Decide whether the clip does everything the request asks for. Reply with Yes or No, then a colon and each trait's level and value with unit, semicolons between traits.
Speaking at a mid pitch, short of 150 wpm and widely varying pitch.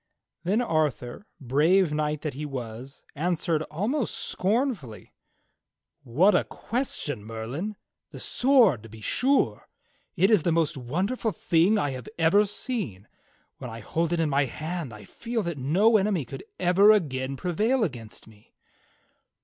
No: medium, 165 Hz; average, 155 wpm; wide, 7.9 semitones